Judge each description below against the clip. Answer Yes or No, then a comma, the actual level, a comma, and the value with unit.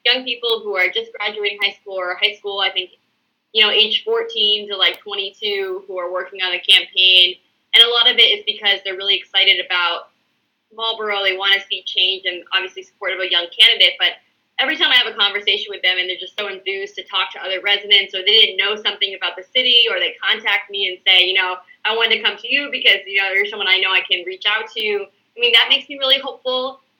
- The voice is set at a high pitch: Yes, high, 200 Hz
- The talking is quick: Yes, fast, 245 wpm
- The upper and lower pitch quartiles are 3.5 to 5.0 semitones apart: No, average, 3.1 semitones